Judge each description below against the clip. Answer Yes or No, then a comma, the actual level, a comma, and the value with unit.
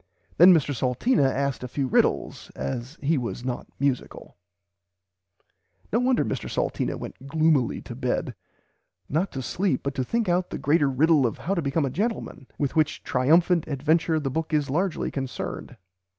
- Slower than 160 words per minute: No, average, 175 wpm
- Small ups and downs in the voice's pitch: No, average, 4.1 semitones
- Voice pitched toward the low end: No, medium, 145 Hz